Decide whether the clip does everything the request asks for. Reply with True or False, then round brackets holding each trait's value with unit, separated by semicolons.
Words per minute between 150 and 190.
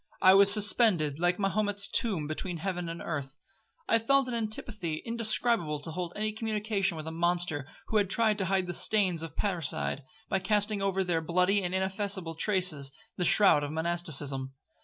True (175 wpm)